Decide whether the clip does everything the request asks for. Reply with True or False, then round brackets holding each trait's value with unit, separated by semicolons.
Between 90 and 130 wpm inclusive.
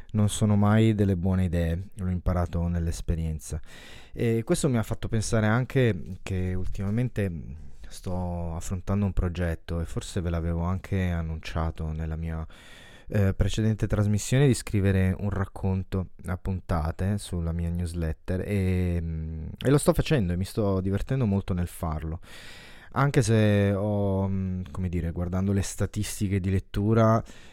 False (140 wpm)